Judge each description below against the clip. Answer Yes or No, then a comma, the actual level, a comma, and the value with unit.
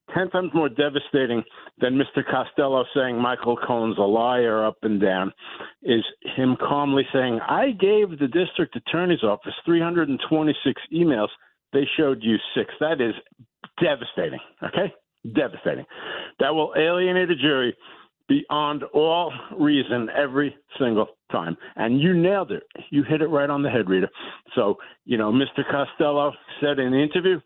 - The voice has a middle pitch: Yes, medium, 145 Hz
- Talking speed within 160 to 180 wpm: No, average, 150 wpm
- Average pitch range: Yes, average, 4.8 semitones